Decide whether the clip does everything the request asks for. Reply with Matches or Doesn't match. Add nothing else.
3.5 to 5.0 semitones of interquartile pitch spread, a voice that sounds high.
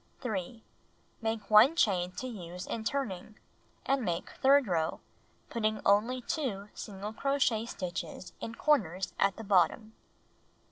Matches